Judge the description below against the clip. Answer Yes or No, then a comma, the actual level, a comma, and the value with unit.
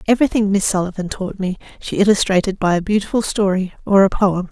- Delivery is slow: No, average, 185 wpm